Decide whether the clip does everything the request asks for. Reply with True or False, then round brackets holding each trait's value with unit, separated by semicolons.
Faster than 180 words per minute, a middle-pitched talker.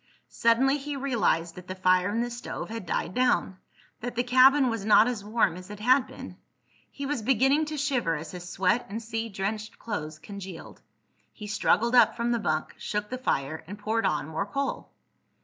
False (190 wpm; 220 Hz)